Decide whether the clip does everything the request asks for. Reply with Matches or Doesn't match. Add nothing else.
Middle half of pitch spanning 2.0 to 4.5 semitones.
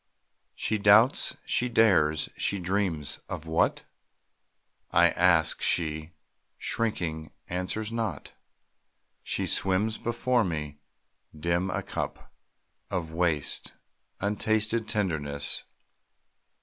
Doesn't match